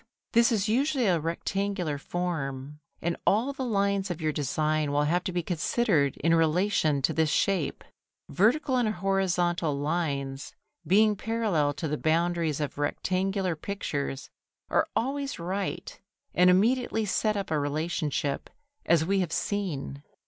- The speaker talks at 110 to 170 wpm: Yes, average, 140 wpm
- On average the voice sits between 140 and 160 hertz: No, medium, 175 Hz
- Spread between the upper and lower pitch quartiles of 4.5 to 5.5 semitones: Yes, average, 4.9 semitones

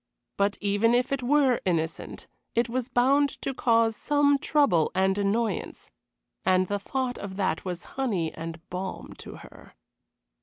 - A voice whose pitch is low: No, high, 220 Hz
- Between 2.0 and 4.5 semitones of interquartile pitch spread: No, wide, 5.5 semitones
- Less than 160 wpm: Yes, average, 150 wpm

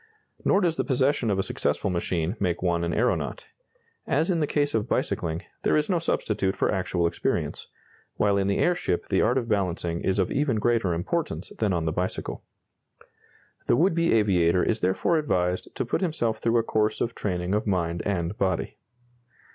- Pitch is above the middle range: No, low, 100 Hz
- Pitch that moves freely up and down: Yes, wide, 6.4 semitones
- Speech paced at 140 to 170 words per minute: No, average, 185 wpm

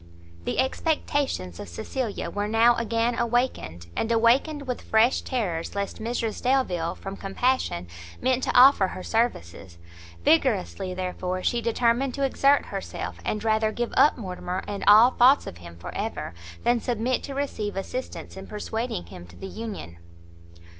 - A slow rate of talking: No, average, 155 wpm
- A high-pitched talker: Yes, high, 225 Hz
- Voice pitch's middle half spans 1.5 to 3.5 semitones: No, average, 5.2 semitones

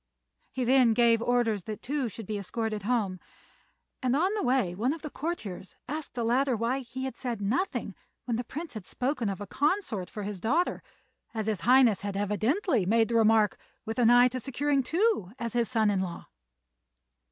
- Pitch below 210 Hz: No, high, 235 Hz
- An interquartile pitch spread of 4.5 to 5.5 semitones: No, average, 3.8 semitones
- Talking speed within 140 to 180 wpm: No, average, 195 wpm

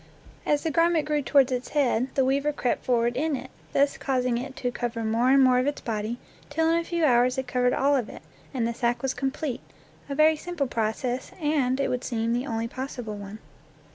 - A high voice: Yes, very high, 260 Hz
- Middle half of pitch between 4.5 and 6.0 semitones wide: No, average, 3.1 semitones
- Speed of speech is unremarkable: No, fast, 220 wpm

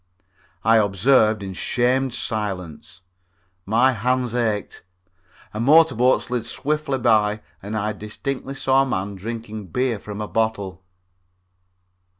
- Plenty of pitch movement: No, average, 3.6 semitones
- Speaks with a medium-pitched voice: No, low, 110 Hz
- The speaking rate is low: Yes, slow, 125 wpm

